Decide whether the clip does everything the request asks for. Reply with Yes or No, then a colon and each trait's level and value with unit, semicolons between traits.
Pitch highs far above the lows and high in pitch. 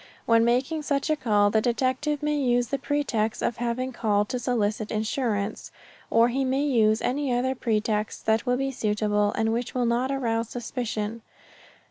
No: average, 3.2 semitones; high, 240 Hz